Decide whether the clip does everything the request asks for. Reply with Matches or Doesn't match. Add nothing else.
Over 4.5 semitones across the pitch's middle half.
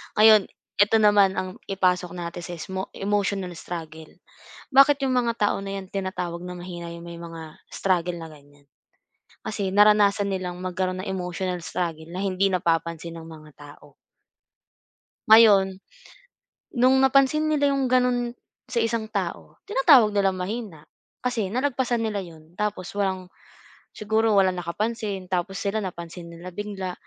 Doesn't match